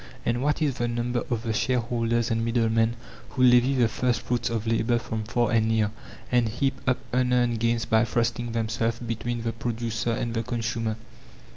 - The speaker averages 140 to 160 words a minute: No, average, 180 wpm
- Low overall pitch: Yes, low, 115 Hz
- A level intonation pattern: Yes, narrow, 1.3 semitones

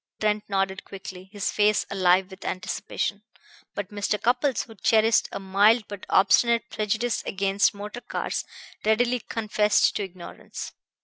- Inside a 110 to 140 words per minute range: Yes, slow, 135 wpm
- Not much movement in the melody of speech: Yes, narrow, 2.2 semitones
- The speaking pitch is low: No, high, 205 Hz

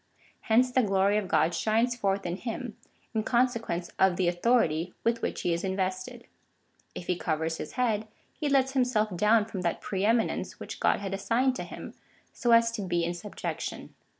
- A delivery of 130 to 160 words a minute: No, average, 185 wpm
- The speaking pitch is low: No, high, 210 Hz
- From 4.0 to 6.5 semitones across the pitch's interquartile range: Yes, average, 4.5 semitones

